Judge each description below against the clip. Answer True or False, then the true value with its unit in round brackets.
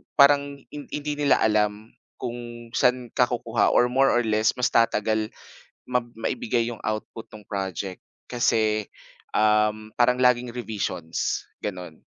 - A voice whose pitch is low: True (115 Hz)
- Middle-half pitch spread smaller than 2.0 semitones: False (2.6 semitones)